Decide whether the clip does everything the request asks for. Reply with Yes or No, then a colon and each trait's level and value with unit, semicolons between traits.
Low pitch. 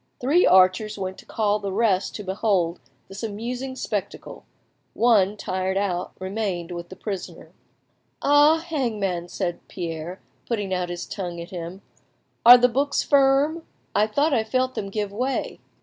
No: high, 205 Hz